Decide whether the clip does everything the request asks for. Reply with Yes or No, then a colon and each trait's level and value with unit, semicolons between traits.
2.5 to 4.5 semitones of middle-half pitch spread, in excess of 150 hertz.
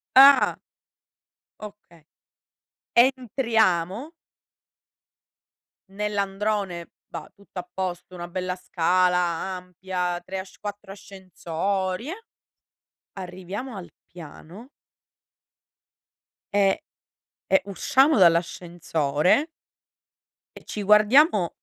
Yes: average, 2.9 semitones; high, 190 Hz